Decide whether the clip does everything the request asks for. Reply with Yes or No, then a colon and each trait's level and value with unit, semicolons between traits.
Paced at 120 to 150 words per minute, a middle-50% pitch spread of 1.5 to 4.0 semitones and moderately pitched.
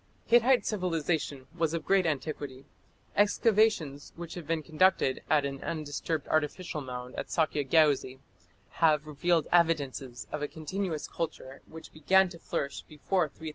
Yes: average, 145 wpm; average, 3.3 semitones; medium, 155 Hz